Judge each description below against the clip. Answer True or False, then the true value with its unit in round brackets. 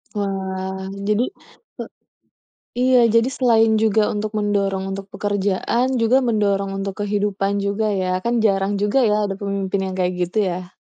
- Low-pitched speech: False (200 Hz)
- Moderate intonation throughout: False (2.0 semitones)